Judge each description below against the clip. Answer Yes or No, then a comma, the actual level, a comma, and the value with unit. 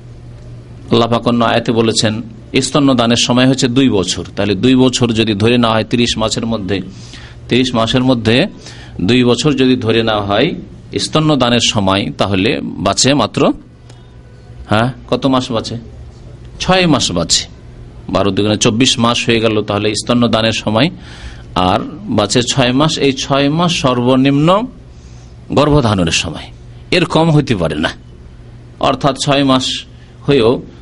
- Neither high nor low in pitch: No, low, 120 Hz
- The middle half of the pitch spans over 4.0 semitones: No, average, 3.7 semitones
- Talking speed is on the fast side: Yes, fast, 135 wpm